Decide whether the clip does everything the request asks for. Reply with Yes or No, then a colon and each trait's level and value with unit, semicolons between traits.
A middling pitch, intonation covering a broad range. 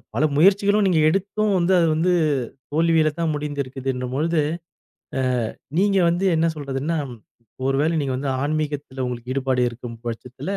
No: medium, 150 Hz; average, 4.1 semitones